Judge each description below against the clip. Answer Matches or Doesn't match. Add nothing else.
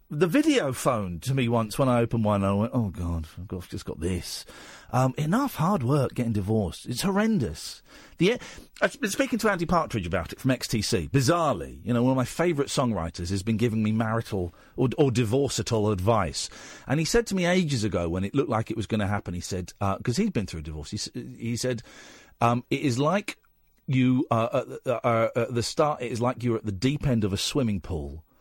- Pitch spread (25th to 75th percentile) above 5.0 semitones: Matches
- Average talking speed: Doesn't match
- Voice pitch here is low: Matches